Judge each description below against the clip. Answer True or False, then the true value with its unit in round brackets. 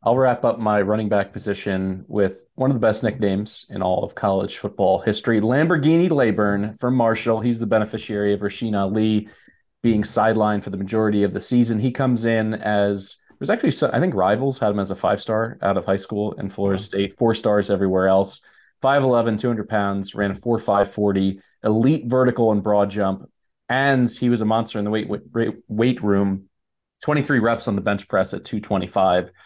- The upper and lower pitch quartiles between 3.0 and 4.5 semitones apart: False (2.5 semitones)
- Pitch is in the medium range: False (105 Hz)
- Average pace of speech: True (190 wpm)